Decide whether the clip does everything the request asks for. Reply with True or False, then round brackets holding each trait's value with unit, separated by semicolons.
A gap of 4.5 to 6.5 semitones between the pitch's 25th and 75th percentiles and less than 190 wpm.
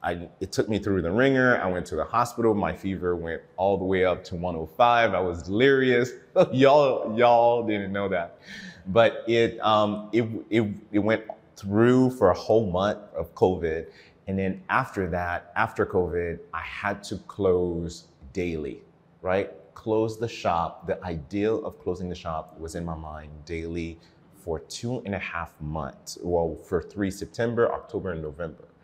True (5.1 semitones; 170 wpm)